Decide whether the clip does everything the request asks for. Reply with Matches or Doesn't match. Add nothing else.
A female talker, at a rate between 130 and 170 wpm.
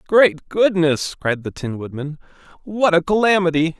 Doesn't match